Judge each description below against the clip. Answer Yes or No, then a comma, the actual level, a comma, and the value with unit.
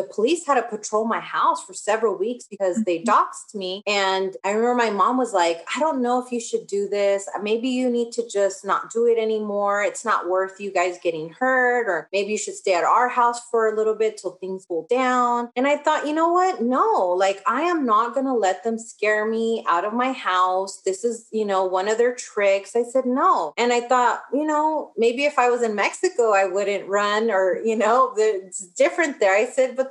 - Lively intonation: No, average, 4.2 semitones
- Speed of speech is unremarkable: No, fast, 230 wpm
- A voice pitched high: Yes, high, 225 Hz